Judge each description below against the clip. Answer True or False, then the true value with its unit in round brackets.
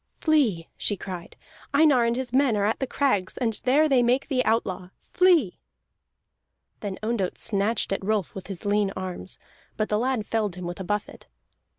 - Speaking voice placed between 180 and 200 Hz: False (215 Hz)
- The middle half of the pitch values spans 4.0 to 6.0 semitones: True (4.7 semitones)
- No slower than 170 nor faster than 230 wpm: True (180 wpm)